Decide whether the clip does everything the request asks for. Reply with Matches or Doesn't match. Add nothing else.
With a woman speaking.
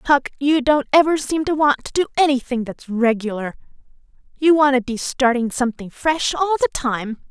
Matches